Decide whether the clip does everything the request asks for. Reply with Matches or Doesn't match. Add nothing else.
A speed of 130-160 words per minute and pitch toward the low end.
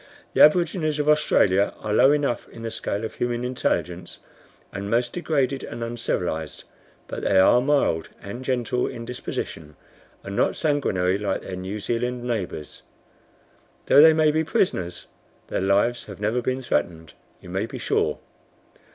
Matches